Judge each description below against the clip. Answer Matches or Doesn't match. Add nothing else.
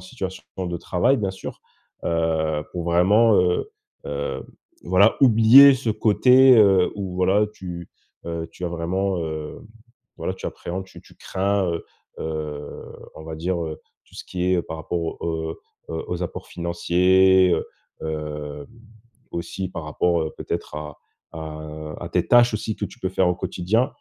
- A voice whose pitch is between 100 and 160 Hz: Doesn't match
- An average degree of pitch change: Matches